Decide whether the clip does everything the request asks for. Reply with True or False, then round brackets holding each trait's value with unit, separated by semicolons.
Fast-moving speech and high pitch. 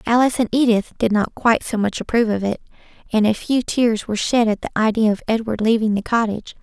True (225 wpm; 220 Hz)